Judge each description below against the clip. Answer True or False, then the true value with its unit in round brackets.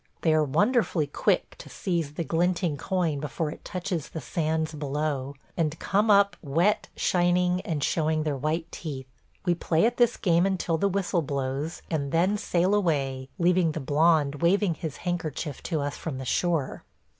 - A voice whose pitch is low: False (165 Hz)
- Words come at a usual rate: True (170 wpm)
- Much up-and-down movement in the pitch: False (3.4 semitones)